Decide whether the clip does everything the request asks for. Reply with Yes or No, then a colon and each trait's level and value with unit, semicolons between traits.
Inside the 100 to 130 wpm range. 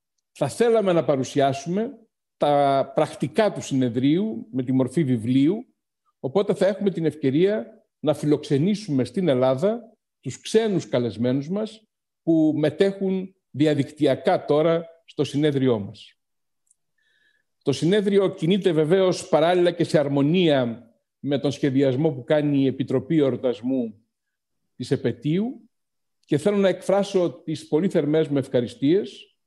Yes: average, 120 wpm